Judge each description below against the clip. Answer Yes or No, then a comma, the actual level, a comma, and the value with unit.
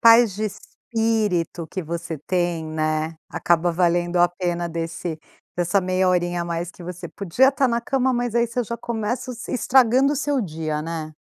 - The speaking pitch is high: No, medium, 180 Hz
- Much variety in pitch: Yes, wide, 5.7 semitones